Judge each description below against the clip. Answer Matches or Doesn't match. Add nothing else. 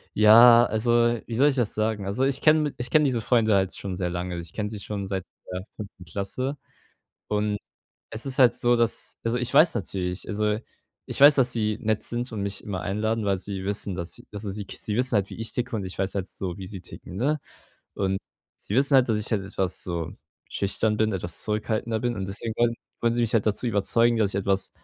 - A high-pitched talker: Doesn't match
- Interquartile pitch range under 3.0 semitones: Doesn't match